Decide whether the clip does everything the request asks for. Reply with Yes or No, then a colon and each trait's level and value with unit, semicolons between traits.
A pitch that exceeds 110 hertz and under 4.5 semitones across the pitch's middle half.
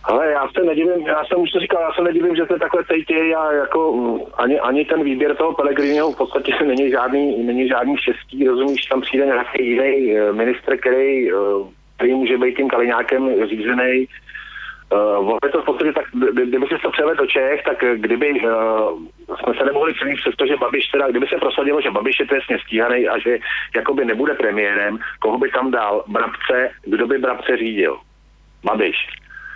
No: medium, 140 Hz; wide, 5.5 semitones